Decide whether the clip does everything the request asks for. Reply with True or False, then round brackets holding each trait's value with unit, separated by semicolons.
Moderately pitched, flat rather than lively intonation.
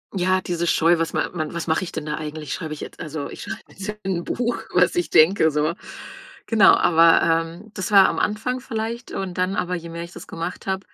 False (175 Hz; 3.1 semitones)